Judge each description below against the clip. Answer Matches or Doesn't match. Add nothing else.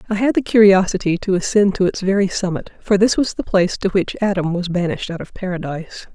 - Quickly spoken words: Matches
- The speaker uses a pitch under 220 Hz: Matches